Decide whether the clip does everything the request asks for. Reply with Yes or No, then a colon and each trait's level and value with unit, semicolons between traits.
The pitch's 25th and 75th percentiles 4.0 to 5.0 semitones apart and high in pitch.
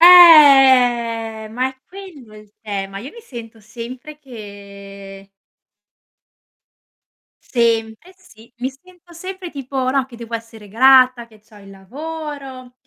Yes: average, 4.3 semitones; high, 245 Hz